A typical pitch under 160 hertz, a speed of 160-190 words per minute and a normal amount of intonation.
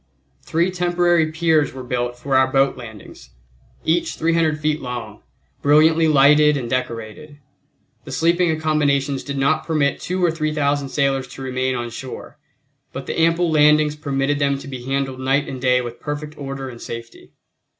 Yes: medium, 140 Hz; average, 165 wpm; average, 3.1 semitones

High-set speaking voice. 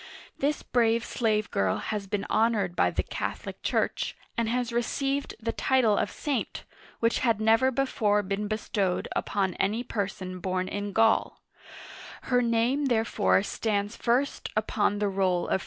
Yes: high, 220 Hz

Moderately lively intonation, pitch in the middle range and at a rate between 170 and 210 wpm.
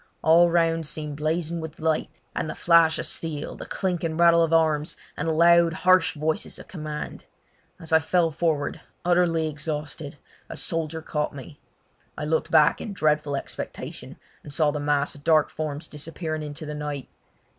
No: narrow, 1.8 semitones; medium, 160 Hz; average, 175 wpm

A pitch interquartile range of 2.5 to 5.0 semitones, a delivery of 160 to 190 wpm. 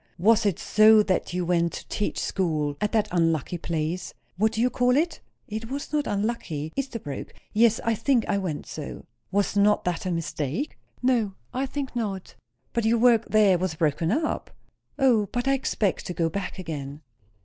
No: wide, 5.6 semitones; average, 180 wpm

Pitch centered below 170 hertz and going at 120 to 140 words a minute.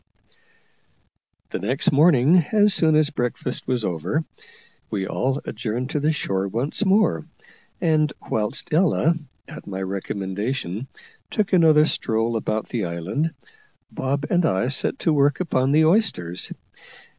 Yes: low, 135 Hz; slow, 135 wpm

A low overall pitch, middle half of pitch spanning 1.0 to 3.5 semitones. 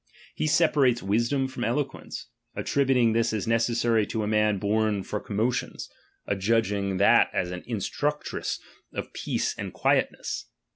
Yes: low, 115 Hz; average, 3.2 semitones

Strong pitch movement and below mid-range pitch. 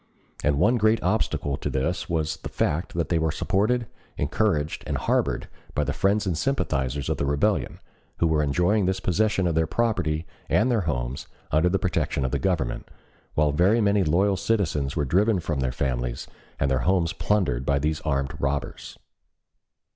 Yes: wide, 5.9 semitones; very low, 80 Hz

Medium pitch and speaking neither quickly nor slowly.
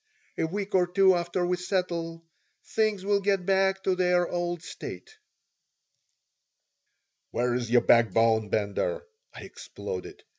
No: medium, 180 Hz; slow, 120 wpm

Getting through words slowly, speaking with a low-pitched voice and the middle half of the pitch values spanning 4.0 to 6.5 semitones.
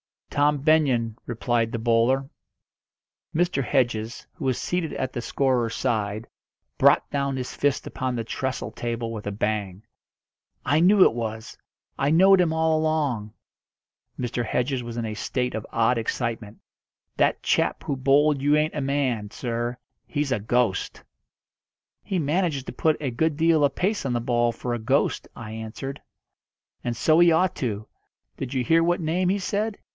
No: average, 170 wpm; low, 130 Hz; average, 4.9 semitones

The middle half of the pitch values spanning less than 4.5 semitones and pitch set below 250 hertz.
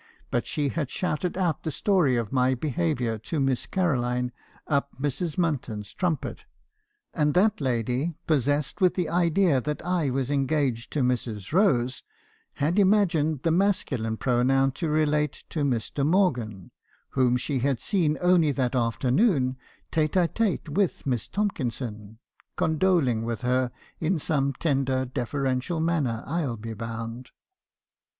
No: average, 5.0 semitones; medium, 140 Hz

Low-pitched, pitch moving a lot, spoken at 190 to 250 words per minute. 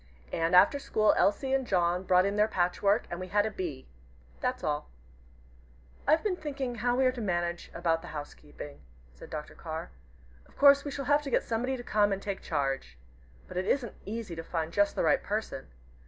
No: high, 200 Hz; wide, 6.5 semitones; average, 200 wpm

